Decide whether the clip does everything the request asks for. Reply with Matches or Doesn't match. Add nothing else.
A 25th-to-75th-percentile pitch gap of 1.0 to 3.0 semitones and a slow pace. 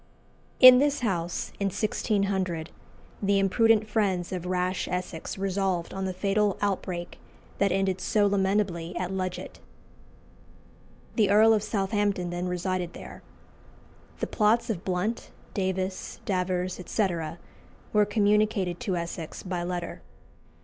Matches